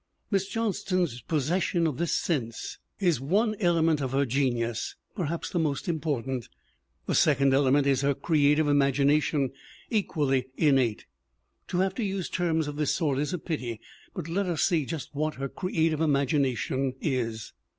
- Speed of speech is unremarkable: Yes, average, 160 wpm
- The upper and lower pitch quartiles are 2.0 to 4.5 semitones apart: Yes, average, 4.0 semitones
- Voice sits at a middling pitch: Yes, medium, 150 Hz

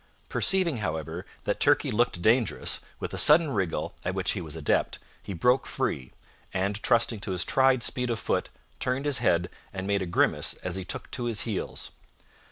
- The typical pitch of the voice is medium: No, low, 105 Hz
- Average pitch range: No, wide, 5.8 semitones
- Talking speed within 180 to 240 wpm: Yes, average, 190 wpm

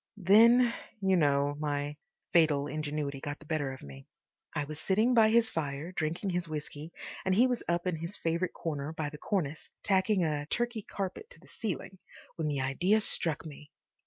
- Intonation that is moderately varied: Yes, average, 4.9 semitones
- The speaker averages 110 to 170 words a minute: No, average, 185 wpm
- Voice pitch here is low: No, medium, 165 Hz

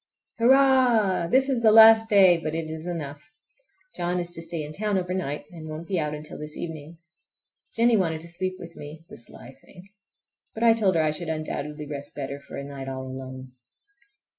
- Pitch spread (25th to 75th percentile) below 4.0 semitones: No, average, 4.7 semitones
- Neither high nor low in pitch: Yes, medium, 165 Hz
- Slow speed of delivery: No, average, 195 wpm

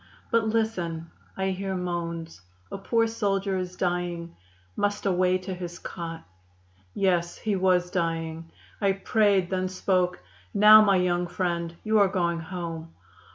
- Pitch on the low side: No, medium, 180 Hz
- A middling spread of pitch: No, narrow, 2.3 semitones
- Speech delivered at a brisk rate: No, average, 140 wpm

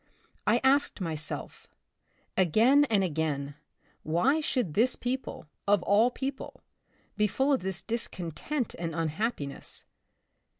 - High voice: Yes, high, 205 Hz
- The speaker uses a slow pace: Yes, slow, 125 wpm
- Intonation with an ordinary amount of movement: No, wide, 7.8 semitones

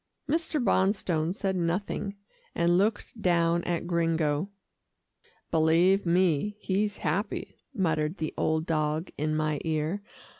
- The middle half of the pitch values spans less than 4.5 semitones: Yes, average, 3.6 semitones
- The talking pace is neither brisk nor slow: No, slow, 115 wpm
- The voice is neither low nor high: Yes, medium, 170 Hz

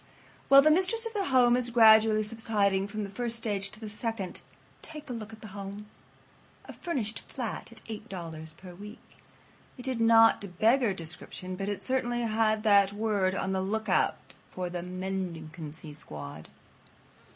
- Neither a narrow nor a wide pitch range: Yes, average, 3.4 semitones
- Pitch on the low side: No, high, 215 Hz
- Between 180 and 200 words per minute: No, average, 165 wpm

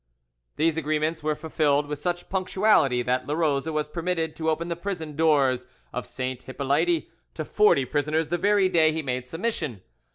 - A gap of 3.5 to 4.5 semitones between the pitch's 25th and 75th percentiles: No, average, 3.1 semitones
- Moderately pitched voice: Yes, medium, 155 Hz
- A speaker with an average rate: Yes, average, 165 wpm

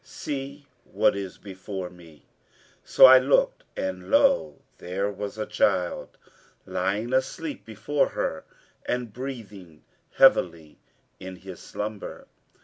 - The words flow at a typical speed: No, slow, 115 wpm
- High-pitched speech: No, low, 100 Hz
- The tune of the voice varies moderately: No, wide, 6.0 semitones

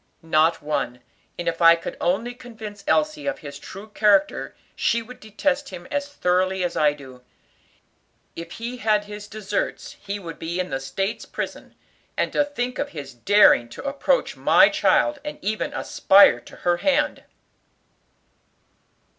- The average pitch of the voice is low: No, high, 205 Hz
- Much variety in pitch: Yes, wide, 6.9 semitones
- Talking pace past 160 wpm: No, average, 155 wpm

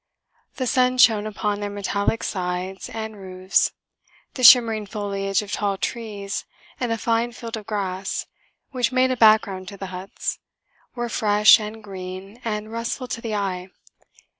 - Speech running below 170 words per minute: Yes, average, 155 wpm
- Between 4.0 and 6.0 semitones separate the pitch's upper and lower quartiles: No, average, 2.7 semitones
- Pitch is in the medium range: No, high, 210 Hz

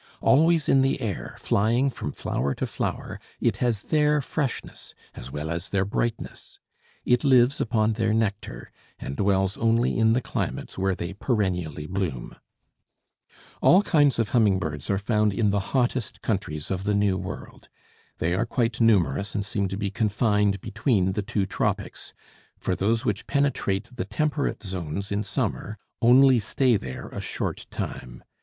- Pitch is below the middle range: Yes, low, 105 Hz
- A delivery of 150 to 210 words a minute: Yes, average, 160 wpm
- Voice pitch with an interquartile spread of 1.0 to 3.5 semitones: No, average, 3.9 semitones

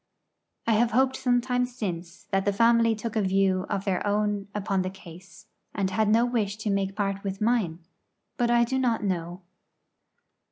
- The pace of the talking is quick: No, average, 175 wpm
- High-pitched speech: Yes, high, 205 Hz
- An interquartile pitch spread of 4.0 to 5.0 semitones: No, average, 3.3 semitones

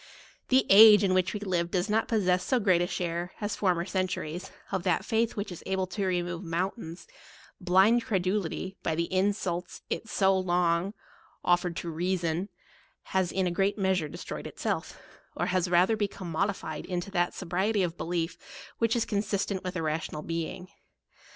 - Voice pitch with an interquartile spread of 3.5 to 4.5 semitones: No, narrow, 2.4 semitones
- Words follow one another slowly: No, average, 185 wpm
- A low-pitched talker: No, medium, 185 Hz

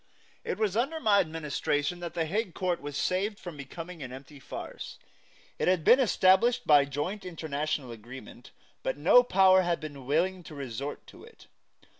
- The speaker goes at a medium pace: Yes, average, 170 wpm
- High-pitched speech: No, medium, 165 Hz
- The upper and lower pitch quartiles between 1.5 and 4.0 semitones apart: No, average, 4.8 semitones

